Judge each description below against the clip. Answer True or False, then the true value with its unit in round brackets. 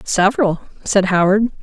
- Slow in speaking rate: True (110 wpm)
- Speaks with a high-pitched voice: True (200 Hz)